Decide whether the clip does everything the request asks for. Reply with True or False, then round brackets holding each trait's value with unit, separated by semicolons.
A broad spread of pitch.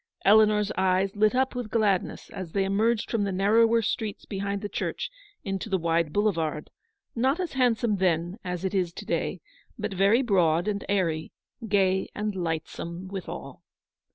False (2.9 semitones)